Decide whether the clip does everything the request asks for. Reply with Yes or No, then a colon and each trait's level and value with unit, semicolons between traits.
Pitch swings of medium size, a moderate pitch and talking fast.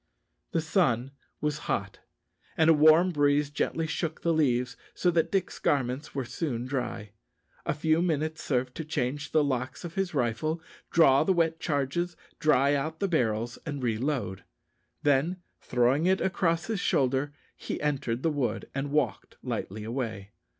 No: average, 4.3 semitones; medium, 145 Hz; average, 160 wpm